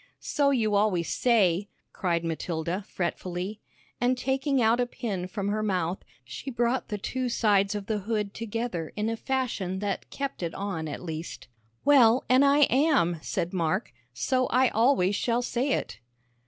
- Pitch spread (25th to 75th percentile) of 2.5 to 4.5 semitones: No, wide, 5.5 semitones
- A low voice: No, high, 210 Hz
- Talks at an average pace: Yes, average, 165 wpm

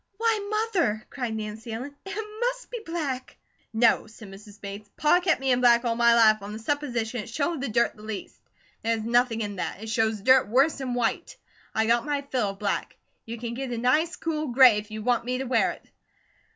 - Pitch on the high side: Yes, high, 240 Hz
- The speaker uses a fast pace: Yes, fast, 215 wpm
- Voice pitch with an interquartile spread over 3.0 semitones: Yes, average, 4.3 semitones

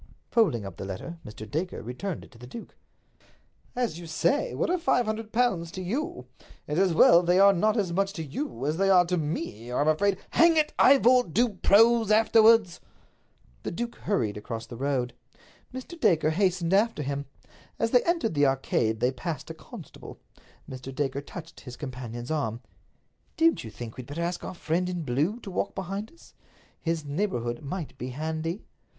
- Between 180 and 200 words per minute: Yes, average, 185 wpm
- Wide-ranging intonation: Yes, wide, 8.1 semitones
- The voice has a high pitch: No, medium, 170 Hz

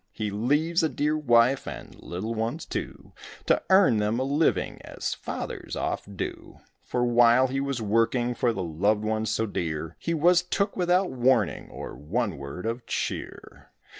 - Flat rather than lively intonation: No, average, 5.1 semitones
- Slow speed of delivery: No, average, 165 wpm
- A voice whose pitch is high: No, low, 120 Hz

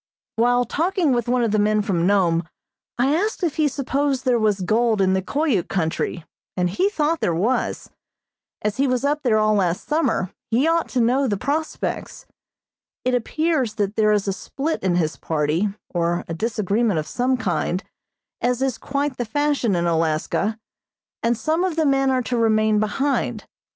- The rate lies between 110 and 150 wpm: No, average, 180 wpm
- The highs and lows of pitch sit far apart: Yes, wide, 6.0 semitones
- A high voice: Yes, high, 230 Hz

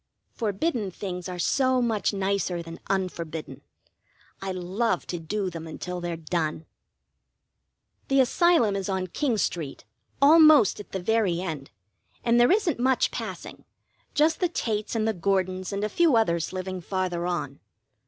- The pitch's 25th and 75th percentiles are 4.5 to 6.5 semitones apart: Yes, average, 5.0 semitones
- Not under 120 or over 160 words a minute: Yes, average, 150 wpm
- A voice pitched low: No, high, 195 Hz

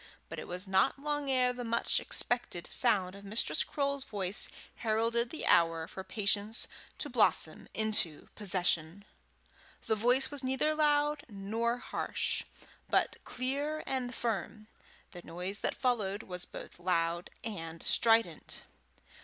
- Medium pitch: No, high, 220 Hz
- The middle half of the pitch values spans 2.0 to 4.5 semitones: No, average, 5.2 semitones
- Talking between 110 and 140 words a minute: Yes, slow, 135 wpm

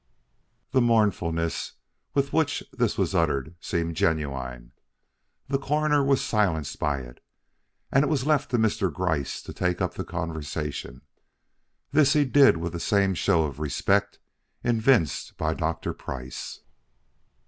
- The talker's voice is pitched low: Yes, very low, 90 Hz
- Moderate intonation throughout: No, wide, 8.9 semitones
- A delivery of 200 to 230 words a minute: No, slow, 135 wpm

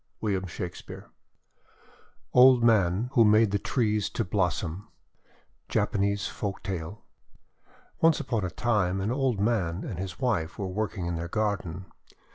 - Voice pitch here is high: No, low, 100 Hz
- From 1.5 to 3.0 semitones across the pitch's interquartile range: No, average, 3.7 semitones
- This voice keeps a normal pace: No, slow, 130 wpm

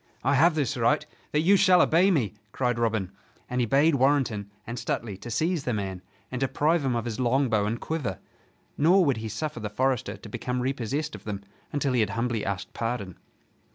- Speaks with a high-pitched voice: No, low, 125 Hz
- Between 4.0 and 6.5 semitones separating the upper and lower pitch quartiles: Yes, average, 4.8 semitones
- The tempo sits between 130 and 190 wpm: No, average, 200 wpm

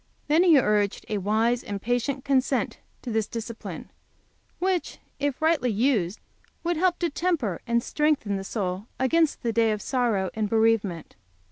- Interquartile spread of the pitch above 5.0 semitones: Yes, wide, 5.4 semitones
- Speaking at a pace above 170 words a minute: No, average, 160 wpm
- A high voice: Yes, high, 235 Hz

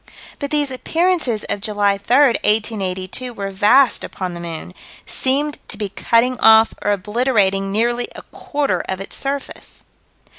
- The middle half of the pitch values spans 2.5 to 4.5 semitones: No, average, 4.9 semitones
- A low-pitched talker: No, high, 220 Hz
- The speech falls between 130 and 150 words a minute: Yes, average, 145 wpm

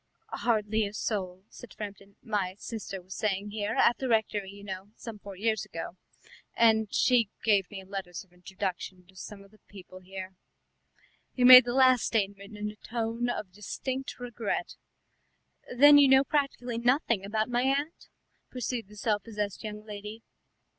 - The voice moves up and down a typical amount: Yes, average, 3.3 semitones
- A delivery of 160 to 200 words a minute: Yes, average, 165 wpm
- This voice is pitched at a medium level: No, high, 210 Hz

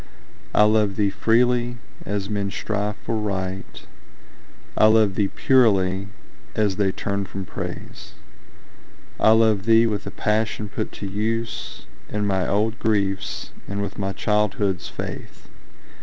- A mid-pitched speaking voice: No, low, 105 Hz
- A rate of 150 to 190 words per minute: No, slow, 135 wpm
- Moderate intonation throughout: No, narrow, 1.9 semitones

